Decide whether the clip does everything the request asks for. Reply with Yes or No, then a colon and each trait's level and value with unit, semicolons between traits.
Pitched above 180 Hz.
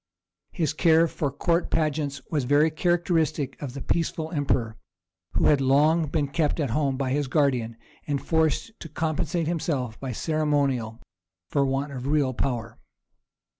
No: medium, 145 Hz